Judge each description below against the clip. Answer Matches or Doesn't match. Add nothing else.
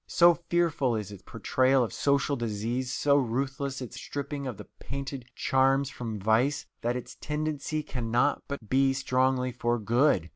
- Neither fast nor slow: Matches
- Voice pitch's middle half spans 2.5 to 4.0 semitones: Matches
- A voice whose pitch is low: Matches